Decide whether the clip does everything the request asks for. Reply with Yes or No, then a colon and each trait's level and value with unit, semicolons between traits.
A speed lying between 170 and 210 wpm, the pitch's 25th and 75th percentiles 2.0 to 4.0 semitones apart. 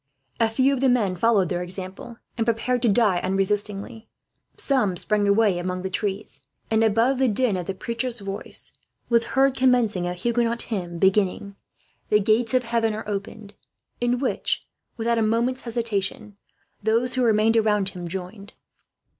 No: average, 160 wpm; average, 3.2 semitones